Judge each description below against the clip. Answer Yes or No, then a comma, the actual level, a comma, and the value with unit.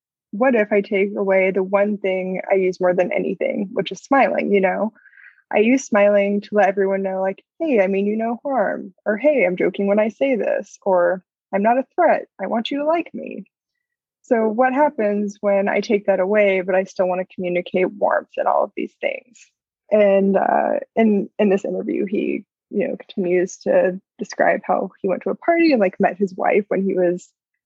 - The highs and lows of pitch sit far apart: No, average, 3.4 semitones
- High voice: Yes, high, 200 Hz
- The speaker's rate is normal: No, fast, 210 wpm